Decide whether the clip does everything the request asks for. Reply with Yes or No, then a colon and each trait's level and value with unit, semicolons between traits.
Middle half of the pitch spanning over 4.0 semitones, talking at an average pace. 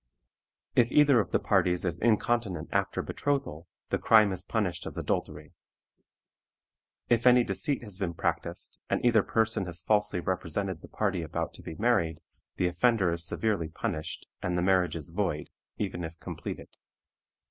Yes: average, 4.7 semitones; average, 160 wpm